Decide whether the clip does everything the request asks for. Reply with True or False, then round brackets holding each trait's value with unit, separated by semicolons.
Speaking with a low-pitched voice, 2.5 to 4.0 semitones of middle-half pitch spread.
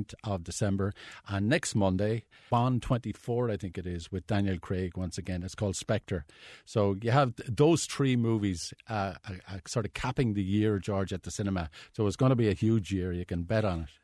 True (100 Hz; 3.2 semitones)